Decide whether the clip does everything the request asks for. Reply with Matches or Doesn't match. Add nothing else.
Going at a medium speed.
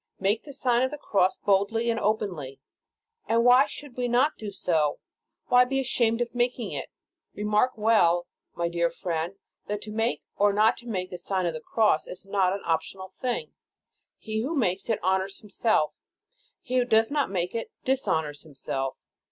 Matches